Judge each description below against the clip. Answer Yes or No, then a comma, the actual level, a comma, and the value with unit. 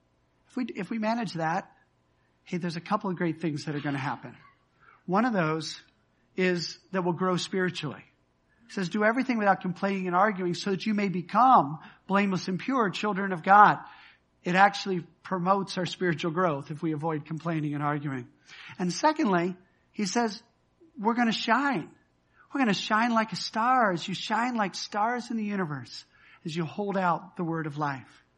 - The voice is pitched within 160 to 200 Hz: Yes, medium, 185 Hz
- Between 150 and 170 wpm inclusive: No, average, 185 wpm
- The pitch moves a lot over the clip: No, average, 4.2 semitones